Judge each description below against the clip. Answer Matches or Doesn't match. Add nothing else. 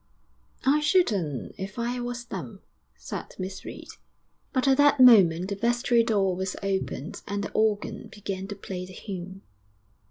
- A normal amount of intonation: Matches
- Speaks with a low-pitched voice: Doesn't match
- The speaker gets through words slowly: Doesn't match